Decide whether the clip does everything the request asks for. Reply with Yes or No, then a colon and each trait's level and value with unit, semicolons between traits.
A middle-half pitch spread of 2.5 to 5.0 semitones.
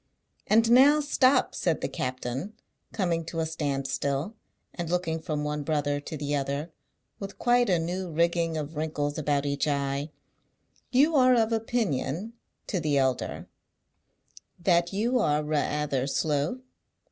No: wide, 5.5 semitones